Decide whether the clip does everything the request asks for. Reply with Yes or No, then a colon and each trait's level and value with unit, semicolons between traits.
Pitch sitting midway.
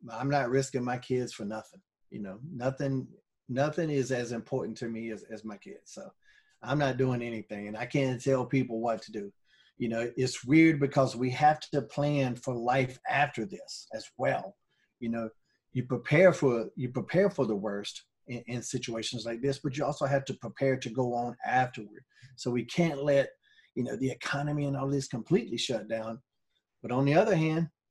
No: low, 130 Hz